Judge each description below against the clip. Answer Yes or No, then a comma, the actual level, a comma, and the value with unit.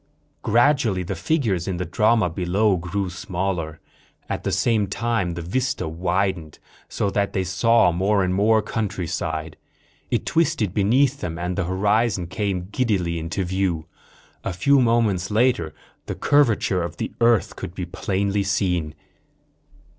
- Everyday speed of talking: Yes, average, 145 wpm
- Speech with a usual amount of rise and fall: Yes, average, 3.9 semitones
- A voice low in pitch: Yes, very low, 95 Hz